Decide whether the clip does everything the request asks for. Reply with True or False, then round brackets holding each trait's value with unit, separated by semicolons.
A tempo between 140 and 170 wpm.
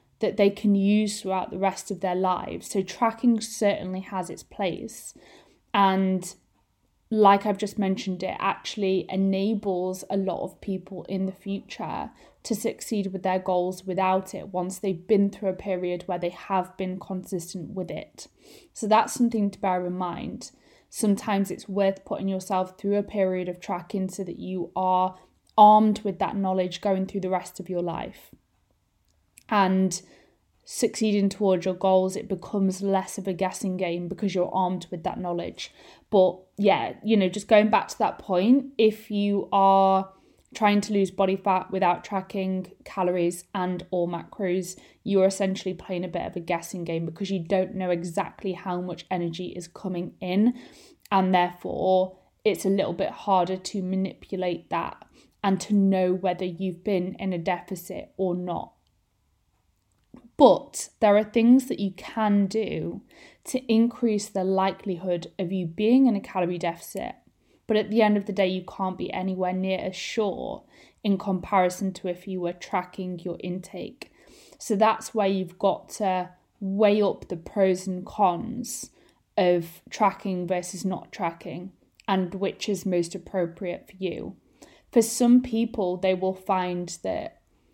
True (165 wpm)